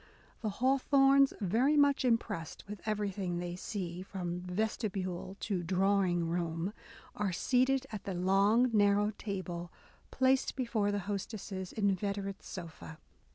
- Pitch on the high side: Yes, high, 200 Hz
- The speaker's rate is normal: No, slow, 130 wpm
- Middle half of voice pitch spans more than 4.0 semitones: No, average, 3.5 semitones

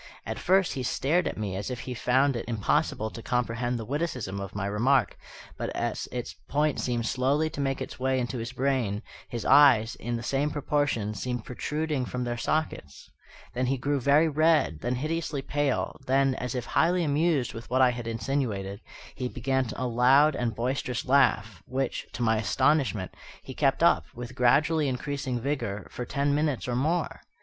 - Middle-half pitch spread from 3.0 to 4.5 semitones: Yes, average, 3.3 semitones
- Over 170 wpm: Yes, average, 185 wpm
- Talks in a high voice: No, low, 130 Hz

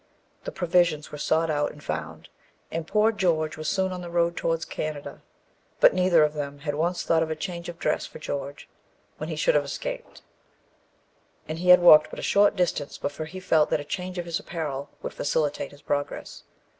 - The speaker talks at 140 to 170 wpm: No, fast, 205 wpm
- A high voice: No, medium, 160 Hz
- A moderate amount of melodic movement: Yes, average, 3.0 semitones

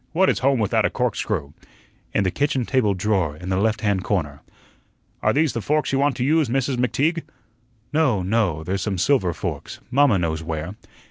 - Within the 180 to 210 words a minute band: Yes, average, 190 wpm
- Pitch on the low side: Yes, low, 110 Hz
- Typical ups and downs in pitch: No, wide, 6.7 semitones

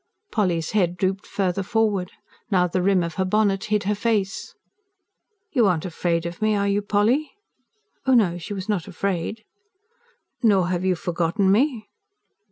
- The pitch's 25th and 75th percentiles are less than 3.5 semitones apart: Yes, average, 2.9 semitones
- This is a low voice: No, high, 195 Hz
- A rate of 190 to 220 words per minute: No, average, 160 wpm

